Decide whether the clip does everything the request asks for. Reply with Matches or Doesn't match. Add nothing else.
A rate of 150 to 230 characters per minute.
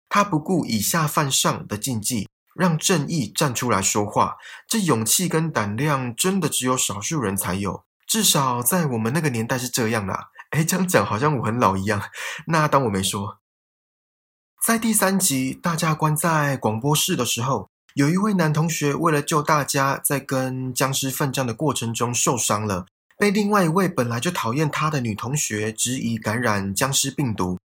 Doesn't match